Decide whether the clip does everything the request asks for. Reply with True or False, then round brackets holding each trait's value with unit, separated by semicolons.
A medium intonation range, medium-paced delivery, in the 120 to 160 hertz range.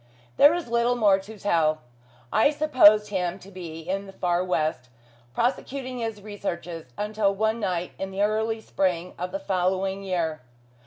False (3.6 semitones; 160 wpm; 195 Hz)